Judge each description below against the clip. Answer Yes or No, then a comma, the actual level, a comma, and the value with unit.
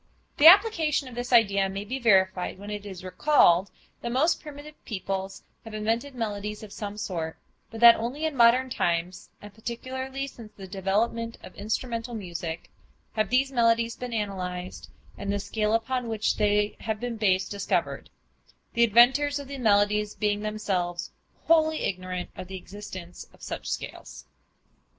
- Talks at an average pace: Yes, average, 160 wpm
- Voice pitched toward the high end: Yes, high, 215 Hz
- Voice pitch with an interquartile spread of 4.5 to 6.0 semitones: No, average, 3.8 semitones